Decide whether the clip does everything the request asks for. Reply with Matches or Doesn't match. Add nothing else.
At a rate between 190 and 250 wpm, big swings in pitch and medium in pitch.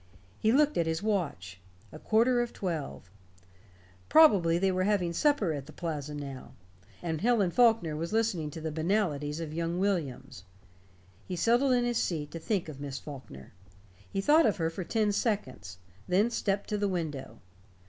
Doesn't match